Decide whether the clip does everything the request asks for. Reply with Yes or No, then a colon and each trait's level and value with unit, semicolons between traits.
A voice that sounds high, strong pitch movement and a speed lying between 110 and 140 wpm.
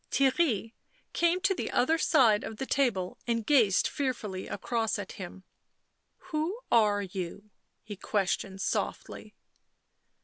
Yes: high, 225 Hz; wide, 5.7 semitones; slow, 135 wpm